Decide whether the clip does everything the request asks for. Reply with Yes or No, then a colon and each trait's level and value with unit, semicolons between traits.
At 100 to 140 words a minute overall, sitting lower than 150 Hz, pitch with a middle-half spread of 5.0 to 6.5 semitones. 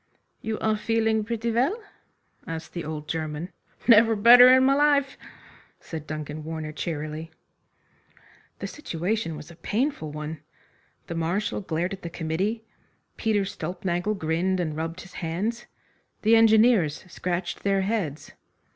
No: slow, 135 wpm; medium, 185 Hz; wide, 5.6 semitones